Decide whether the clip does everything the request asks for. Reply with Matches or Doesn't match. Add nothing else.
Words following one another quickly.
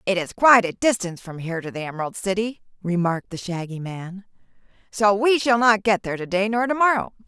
Matches